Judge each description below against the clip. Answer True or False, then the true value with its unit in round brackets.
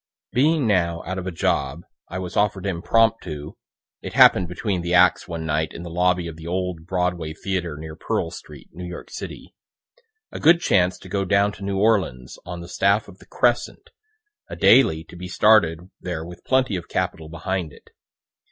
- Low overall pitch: True (90 Hz)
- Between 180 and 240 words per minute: True (190 wpm)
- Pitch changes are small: False (3.0 semitones)